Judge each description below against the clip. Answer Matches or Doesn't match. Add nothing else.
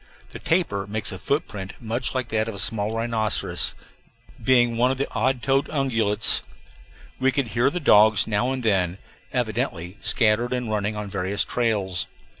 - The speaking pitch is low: Matches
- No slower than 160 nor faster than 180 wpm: Matches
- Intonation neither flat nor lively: Matches